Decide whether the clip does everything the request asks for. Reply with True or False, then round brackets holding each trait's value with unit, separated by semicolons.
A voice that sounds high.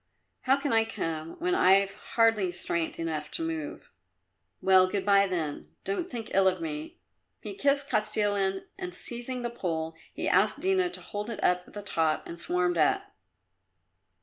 True (195 Hz)